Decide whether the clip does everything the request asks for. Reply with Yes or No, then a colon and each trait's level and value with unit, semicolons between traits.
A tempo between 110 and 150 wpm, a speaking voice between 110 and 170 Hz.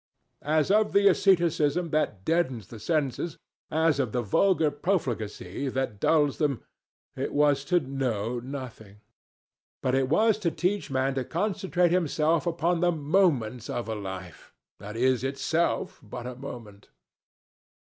Yes: average, 140 wpm; medium, 140 Hz